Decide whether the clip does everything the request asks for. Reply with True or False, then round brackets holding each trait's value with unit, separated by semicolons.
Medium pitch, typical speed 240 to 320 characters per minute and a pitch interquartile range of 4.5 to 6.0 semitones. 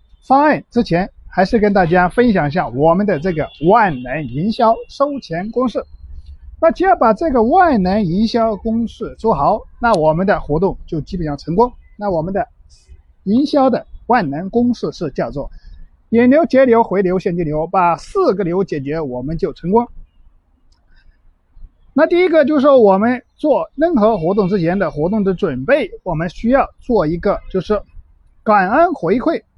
False (210 Hz; 245 characters per minute; 5.4 semitones)